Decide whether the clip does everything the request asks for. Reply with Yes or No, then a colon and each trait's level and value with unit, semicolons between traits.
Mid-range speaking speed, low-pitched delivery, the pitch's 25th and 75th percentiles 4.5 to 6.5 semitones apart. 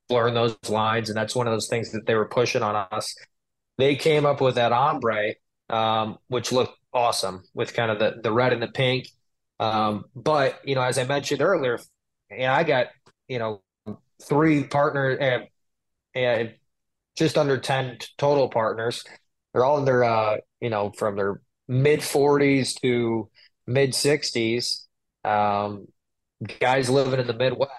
No: average, 165 wpm; low, 125 Hz; average, 3.8 semitones